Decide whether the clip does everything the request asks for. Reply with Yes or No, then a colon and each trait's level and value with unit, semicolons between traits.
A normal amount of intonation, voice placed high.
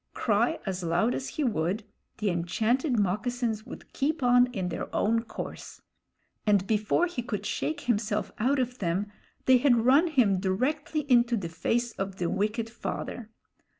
Yes: average, 3.9 semitones; high, 230 Hz